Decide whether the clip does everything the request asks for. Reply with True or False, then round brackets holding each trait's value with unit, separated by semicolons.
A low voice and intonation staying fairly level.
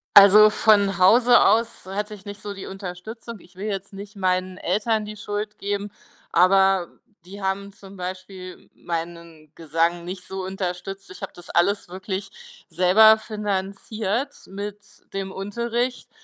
False (195 Hz; 2.2 semitones)